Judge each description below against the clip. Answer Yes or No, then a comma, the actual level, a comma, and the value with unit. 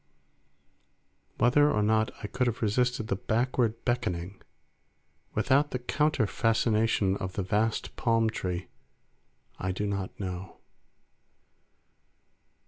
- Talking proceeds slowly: Yes, slow, 110 wpm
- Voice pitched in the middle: No, low, 110 Hz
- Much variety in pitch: No, average, 3.7 semitones